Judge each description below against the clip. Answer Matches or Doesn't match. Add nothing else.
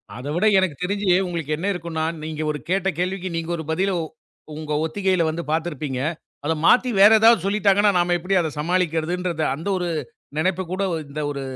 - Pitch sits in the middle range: Matches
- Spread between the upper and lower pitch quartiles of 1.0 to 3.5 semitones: Matches